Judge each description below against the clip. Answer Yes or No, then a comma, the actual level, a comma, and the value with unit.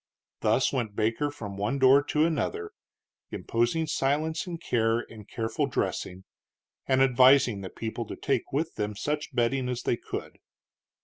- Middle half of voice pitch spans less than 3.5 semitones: No, average, 4.7 semitones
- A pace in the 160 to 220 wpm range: No, average, 150 wpm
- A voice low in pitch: Yes, low, 125 Hz